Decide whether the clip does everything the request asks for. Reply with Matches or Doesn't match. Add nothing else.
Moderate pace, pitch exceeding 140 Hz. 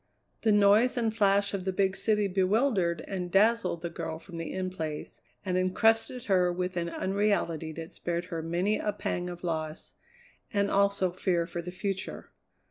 Matches